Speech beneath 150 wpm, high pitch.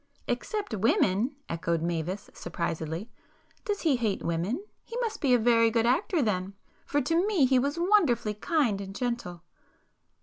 Yes: average, 140 wpm; high, 235 Hz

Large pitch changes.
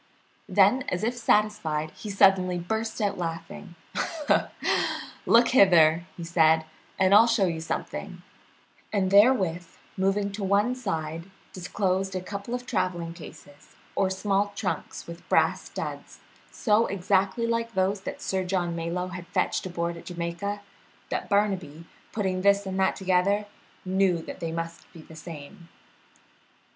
No: average, 3.1 semitones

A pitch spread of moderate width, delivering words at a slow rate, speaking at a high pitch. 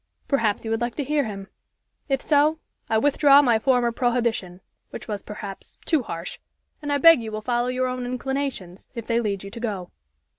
No: average, 4.1 semitones; average, 195 wpm; high, 240 Hz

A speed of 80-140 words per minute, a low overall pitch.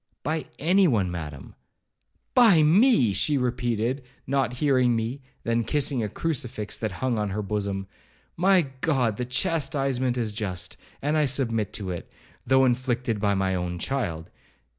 No: average, 150 wpm; low, 125 Hz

